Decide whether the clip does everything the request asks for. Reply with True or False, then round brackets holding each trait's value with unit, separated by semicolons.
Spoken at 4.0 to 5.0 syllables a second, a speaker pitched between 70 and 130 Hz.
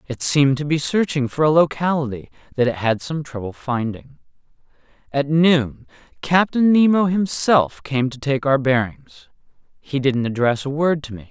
False (4.7 syllables/s; 140 Hz)